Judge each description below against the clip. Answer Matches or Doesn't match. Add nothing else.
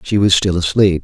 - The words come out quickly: Matches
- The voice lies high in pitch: Doesn't match